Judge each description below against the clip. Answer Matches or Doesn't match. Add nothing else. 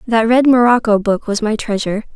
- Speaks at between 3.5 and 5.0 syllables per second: Doesn't match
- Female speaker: Matches